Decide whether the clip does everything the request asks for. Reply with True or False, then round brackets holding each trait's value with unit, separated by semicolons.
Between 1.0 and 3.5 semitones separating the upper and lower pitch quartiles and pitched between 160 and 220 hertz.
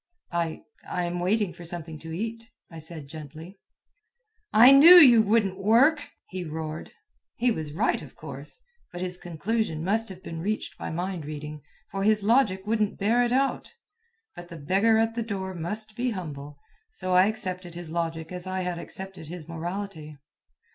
False (4.9 semitones; 185 Hz)